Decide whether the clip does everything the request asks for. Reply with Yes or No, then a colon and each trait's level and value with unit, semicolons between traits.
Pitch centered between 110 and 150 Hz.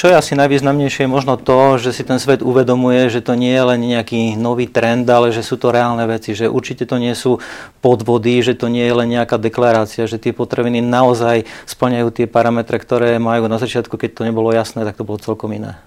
Yes: low, 120 Hz